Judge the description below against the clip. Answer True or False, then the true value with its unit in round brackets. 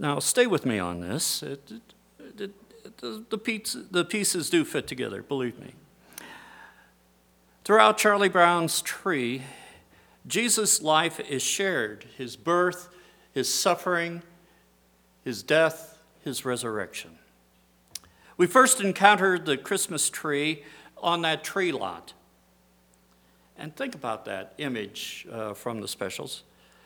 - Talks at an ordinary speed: False (115 wpm)